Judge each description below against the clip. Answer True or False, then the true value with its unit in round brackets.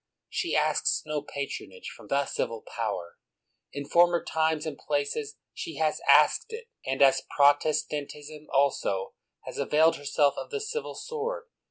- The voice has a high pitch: False (150 Hz)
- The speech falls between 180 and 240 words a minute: False (145 wpm)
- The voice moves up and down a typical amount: True (3.5 semitones)